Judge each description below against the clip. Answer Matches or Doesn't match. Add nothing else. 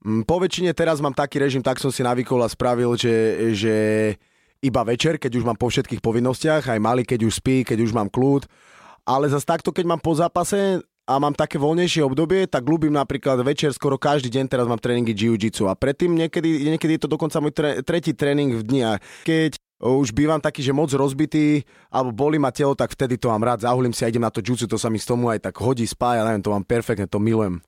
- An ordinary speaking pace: Doesn't match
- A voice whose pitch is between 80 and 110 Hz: Doesn't match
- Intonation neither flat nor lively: Matches